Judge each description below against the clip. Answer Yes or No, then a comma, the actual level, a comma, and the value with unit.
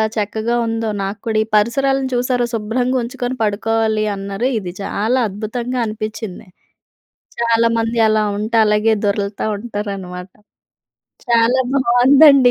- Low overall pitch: No, high, 225 Hz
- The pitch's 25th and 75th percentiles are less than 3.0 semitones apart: Yes, narrow, 2.6 semitones